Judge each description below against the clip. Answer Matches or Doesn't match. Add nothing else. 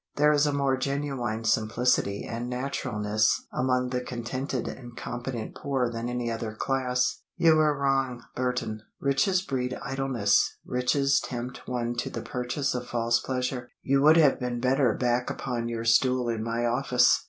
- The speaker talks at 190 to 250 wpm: Doesn't match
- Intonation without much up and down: Matches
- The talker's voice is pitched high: Doesn't match